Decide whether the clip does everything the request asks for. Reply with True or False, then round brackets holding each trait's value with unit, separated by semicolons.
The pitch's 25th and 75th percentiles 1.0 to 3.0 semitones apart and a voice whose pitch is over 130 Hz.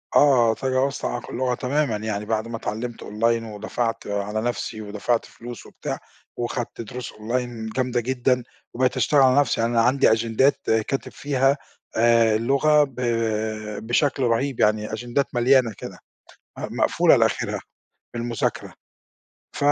False (2.6 semitones; 120 Hz)